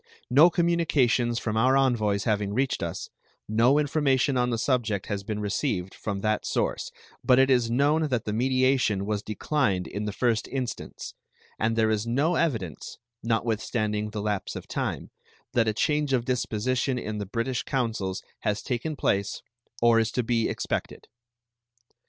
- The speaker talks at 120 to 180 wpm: Yes, average, 160 wpm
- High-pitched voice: No, low, 115 Hz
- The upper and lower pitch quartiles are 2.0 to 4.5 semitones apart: Yes, average, 3.8 semitones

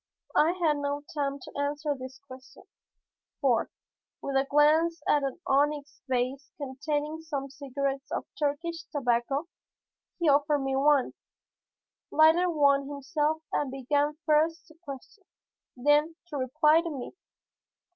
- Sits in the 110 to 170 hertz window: No, very high, 290 Hz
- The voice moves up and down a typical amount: No, narrow, 2.1 semitones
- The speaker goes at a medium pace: No, slow, 130 wpm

